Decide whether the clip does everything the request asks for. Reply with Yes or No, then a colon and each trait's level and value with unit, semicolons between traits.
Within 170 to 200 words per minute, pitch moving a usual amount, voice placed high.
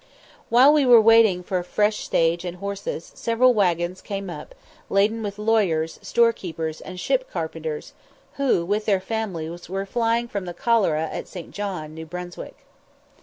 No: average, 160 wpm; average, 4.6 semitones; high, 195 Hz